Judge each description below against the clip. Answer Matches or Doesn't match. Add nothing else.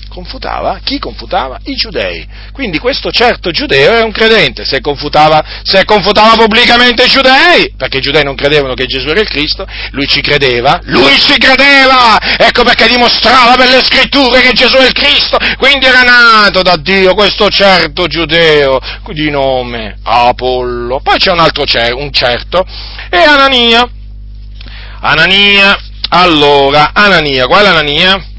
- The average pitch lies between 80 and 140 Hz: Doesn't match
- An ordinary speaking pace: Matches